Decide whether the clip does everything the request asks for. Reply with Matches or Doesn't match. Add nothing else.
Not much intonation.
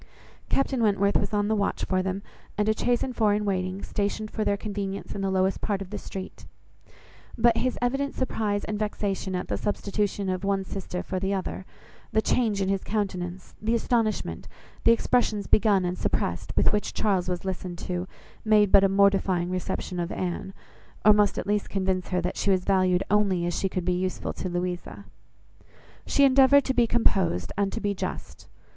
Matches